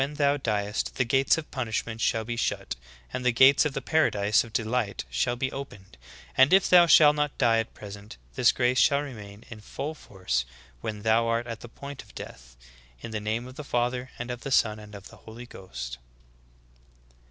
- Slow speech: No, average, 200 wpm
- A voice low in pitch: Yes, low, 115 Hz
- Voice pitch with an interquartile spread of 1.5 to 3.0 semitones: No, average, 4.1 semitones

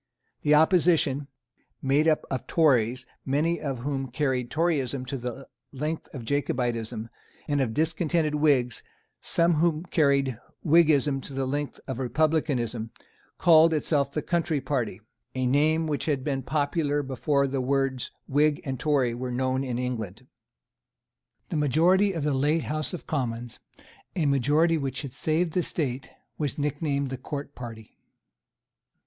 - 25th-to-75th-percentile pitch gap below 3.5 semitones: Yes, average, 3.1 semitones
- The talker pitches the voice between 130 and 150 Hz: Yes, medium, 140 Hz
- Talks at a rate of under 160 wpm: Yes, average, 145 wpm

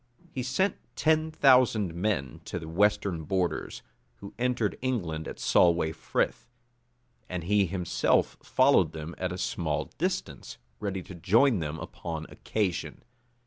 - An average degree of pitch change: No, wide, 6.1 semitones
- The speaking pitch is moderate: No, very low, 95 Hz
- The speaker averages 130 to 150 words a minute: Yes, slow, 135 wpm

